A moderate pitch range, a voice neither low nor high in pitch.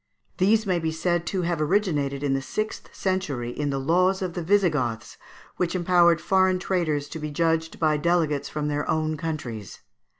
Yes: average, 3.7 semitones; medium, 165 Hz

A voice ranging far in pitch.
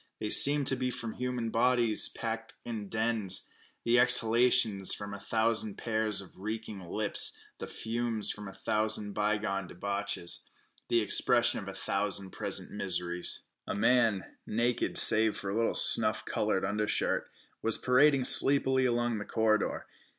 No: average, 2.7 semitones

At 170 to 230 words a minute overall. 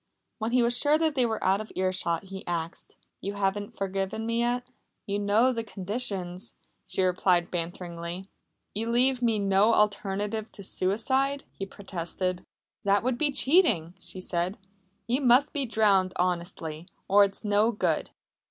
No: average, 155 wpm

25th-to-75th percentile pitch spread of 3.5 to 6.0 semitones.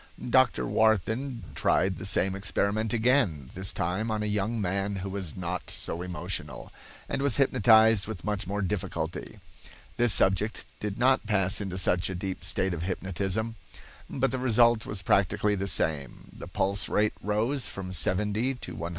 No: average, 3.1 semitones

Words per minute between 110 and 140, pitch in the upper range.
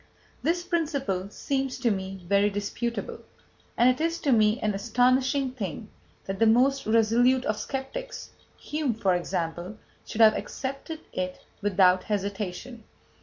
Yes: slow, 135 wpm; high, 225 Hz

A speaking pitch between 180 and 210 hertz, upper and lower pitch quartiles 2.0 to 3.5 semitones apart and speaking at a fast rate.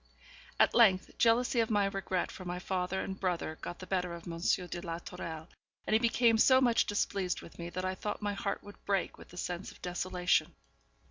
Yes: medium, 185 Hz; average, 2.7 semitones; fast, 210 wpm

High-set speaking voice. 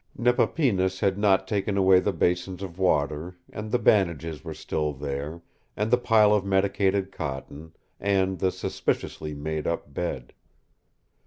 No: very low, 95 Hz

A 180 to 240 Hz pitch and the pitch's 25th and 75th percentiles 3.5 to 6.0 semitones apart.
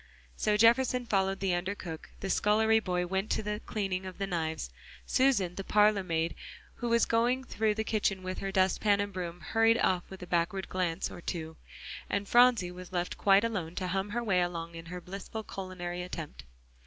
No: high, 190 Hz; average, 3.1 semitones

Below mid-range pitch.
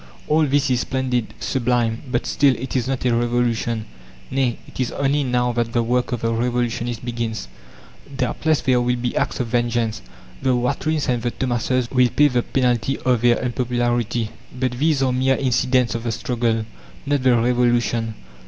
Yes: low, 125 Hz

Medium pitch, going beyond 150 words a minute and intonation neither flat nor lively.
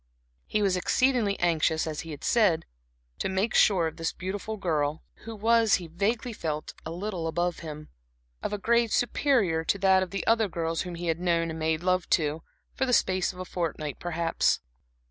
Yes: medium, 180 Hz; average, 195 wpm; average, 4.2 semitones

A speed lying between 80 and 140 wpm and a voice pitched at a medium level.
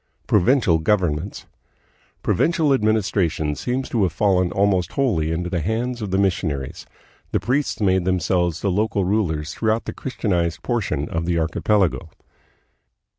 No: slow, 135 wpm; very low, 95 Hz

